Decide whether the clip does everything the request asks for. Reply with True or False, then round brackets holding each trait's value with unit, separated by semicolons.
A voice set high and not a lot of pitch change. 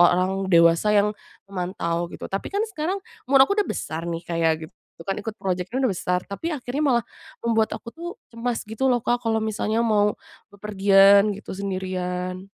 False (200 Hz; 4.4 semitones)